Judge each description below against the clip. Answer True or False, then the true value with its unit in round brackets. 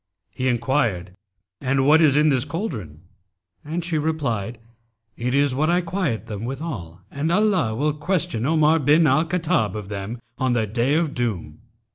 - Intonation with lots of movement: True (5.7 semitones)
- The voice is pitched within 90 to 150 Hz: True (140 Hz)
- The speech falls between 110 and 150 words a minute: False (165 wpm)